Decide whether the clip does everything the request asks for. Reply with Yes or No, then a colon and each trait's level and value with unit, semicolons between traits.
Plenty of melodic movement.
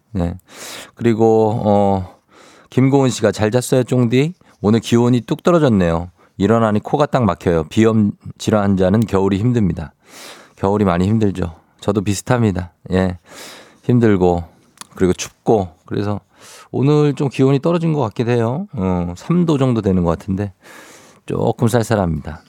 No: average, 5.0 semitones